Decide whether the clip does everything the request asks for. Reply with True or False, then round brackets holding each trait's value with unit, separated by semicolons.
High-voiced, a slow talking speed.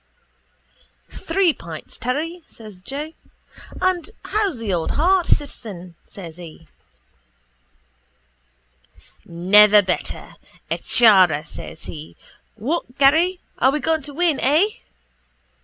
True (250 Hz; 105 wpm)